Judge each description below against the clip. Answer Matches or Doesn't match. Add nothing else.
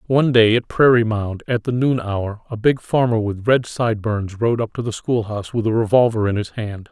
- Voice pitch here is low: Matches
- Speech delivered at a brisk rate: Matches